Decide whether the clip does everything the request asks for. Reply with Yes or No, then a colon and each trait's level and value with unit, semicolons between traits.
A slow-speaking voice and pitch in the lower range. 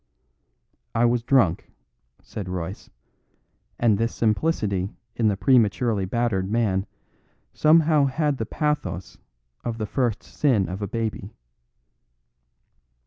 Yes: slow, 110 wpm; low, 115 Hz